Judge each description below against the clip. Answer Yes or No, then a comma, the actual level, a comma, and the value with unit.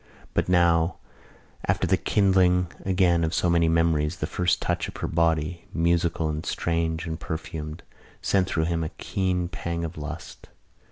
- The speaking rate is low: No, average, 160 wpm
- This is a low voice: Yes, very low, 85 Hz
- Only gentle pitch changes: Yes, narrow, 1.7 semitones